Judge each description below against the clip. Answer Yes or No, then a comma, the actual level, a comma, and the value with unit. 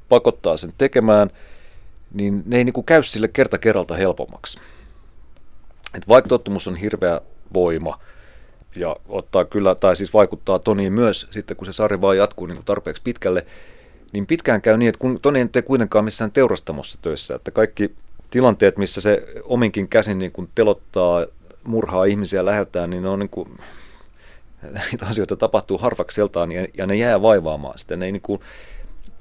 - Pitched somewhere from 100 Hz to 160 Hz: Yes, low, 105 Hz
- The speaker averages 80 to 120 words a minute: No, fast, 155 wpm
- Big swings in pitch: No, average, 3.3 semitones